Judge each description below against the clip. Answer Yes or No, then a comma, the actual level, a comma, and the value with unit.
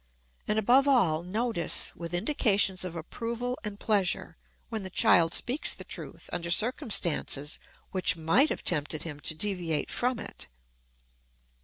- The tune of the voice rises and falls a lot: Yes, wide, 5.7 semitones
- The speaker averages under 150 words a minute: Yes, average, 140 wpm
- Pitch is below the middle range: No, high, 190 Hz